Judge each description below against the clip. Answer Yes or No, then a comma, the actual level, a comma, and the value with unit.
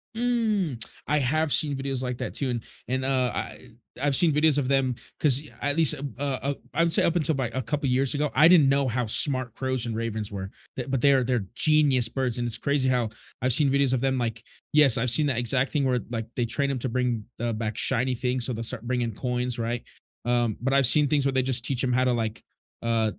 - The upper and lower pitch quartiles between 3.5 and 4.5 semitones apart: No, average, 2.8 semitones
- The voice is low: Yes, low, 130 Hz